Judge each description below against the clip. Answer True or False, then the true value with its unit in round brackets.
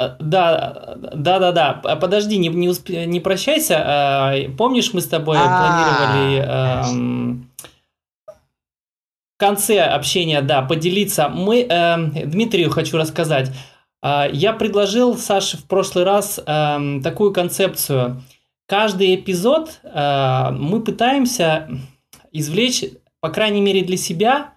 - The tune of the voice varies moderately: False (5.8 semitones)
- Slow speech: True (95 wpm)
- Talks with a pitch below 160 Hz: False (170 Hz)